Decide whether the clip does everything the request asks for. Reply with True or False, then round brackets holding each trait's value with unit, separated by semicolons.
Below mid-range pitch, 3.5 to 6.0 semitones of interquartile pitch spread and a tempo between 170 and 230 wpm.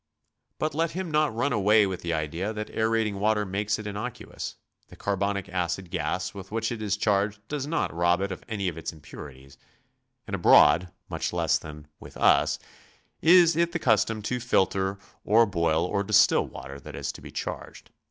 True (100 Hz; 4.1 semitones; 190 wpm)